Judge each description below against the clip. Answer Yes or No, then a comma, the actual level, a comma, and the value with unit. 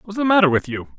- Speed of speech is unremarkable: No, fast, 305 wpm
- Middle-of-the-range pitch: Yes, medium, 180 Hz